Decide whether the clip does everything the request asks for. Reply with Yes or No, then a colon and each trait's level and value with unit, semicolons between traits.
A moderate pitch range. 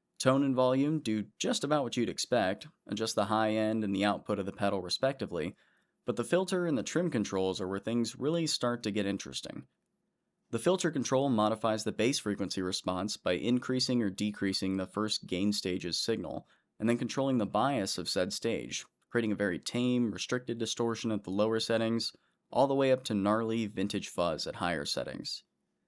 Yes: average, 3.6 semitones